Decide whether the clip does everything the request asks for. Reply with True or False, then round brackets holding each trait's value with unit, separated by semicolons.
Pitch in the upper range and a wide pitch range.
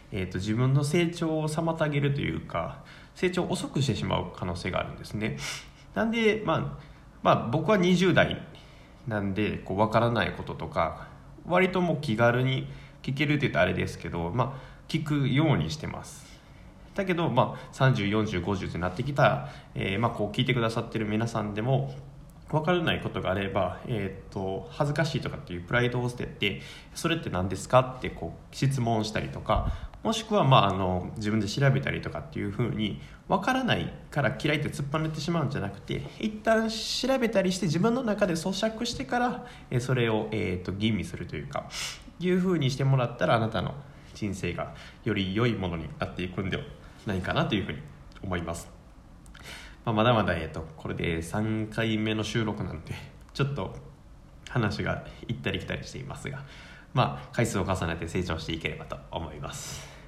False (120 Hz; 8.0 semitones)